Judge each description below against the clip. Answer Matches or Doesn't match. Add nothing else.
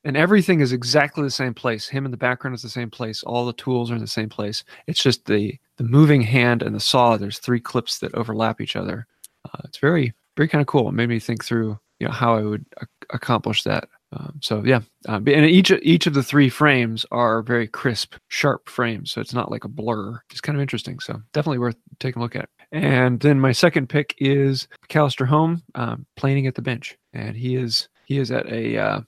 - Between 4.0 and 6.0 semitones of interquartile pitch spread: Doesn't match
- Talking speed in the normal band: Doesn't match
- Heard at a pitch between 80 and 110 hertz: Doesn't match